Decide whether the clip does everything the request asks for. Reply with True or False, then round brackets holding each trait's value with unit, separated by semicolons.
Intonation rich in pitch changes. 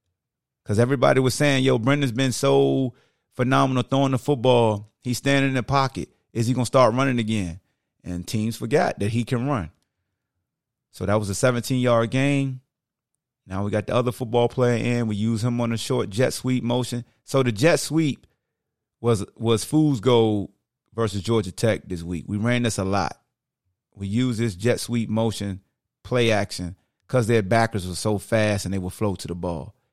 False (3.7 semitones)